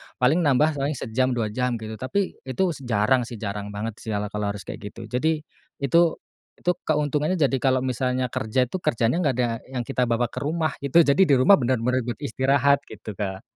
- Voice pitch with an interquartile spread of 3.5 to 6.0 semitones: Yes, average, 3.8 semitones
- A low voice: Yes, low, 125 Hz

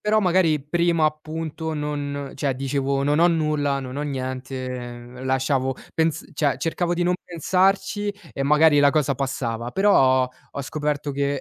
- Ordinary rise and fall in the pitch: Yes, average, 3.2 semitones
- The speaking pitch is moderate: Yes, medium, 145 Hz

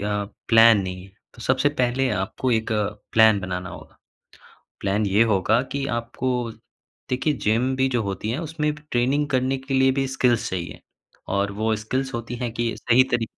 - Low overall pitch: Yes, low, 120 Hz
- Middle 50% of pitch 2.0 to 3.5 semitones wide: No, average, 3.9 semitones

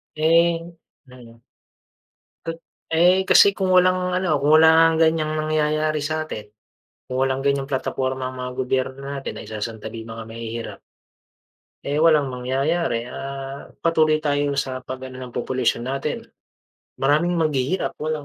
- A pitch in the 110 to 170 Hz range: Yes, medium, 140 Hz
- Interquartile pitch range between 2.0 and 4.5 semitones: Yes, average, 3.5 semitones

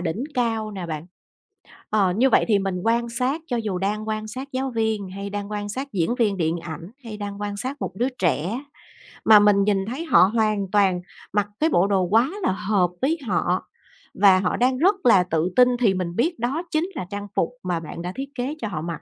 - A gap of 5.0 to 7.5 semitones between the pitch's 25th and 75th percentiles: No, average, 4.5 semitones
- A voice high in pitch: Yes, high, 205 Hz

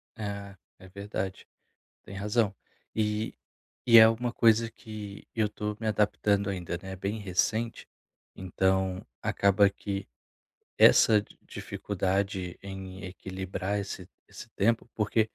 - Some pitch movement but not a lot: No, narrow, 2.1 semitones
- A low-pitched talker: Yes, low, 100 Hz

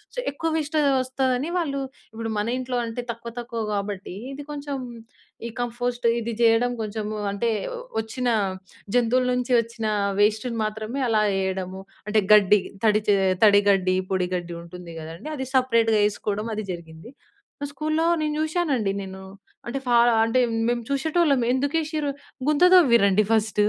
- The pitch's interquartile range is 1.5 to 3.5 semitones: No, average, 4.3 semitones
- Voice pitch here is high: Yes, high, 230 Hz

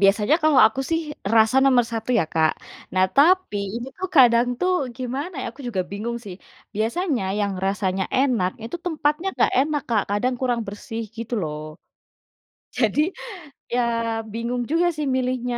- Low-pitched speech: No, high, 240 Hz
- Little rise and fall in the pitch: No, average, 5.0 semitones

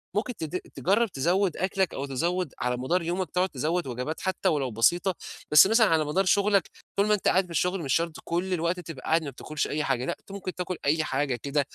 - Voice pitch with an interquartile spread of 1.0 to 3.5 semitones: No, average, 4.4 semitones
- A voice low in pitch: No, medium, 170 Hz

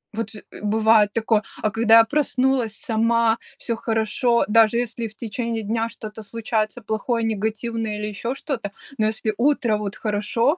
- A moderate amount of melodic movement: No, narrow, 1.5 semitones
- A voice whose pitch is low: No, high, 225 Hz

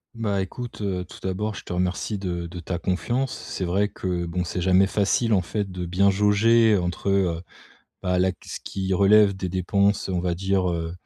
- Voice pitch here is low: Yes, very low, 95 Hz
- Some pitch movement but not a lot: No, narrow, 2.1 semitones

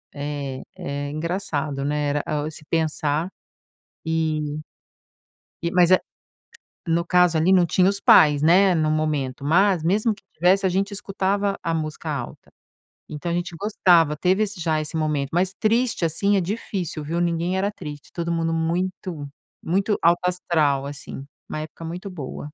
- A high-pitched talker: No, medium, 165 Hz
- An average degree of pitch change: Yes, average, 3.5 semitones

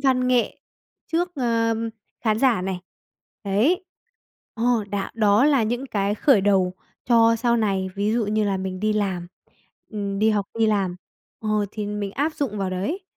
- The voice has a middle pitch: No, high, 215 Hz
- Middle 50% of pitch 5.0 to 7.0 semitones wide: No, average, 3.4 semitones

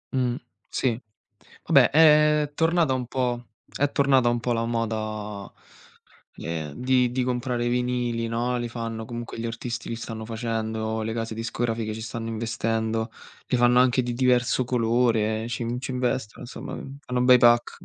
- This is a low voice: Yes, low, 120 Hz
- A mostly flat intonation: Yes, narrow, 1.8 semitones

